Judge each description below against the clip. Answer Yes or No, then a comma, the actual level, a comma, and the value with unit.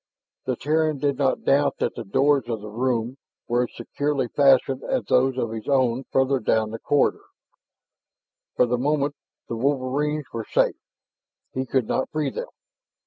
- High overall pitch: No, low, 130 Hz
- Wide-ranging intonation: No, average, 3.0 semitones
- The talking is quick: No, average, 165 wpm